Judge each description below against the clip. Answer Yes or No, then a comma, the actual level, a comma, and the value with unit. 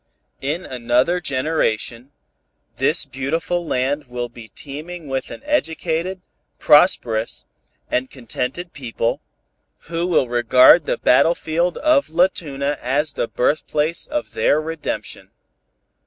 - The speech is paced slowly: Yes, slow, 110 wpm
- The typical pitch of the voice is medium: Yes, medium, 150 Hz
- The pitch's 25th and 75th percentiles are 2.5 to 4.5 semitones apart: No, average, 5.0 semitones